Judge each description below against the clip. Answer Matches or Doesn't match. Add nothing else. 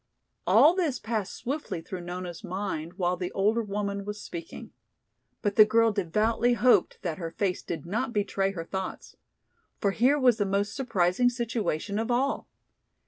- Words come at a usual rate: Matches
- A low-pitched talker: Doesn't match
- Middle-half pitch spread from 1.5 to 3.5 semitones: Doesn't match